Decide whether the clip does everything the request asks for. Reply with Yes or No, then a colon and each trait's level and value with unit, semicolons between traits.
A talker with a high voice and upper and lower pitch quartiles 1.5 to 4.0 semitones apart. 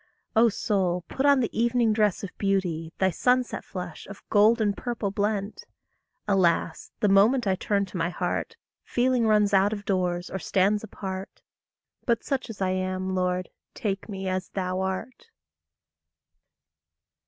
Yes: high, 200 Hz; average, 2.8 semitones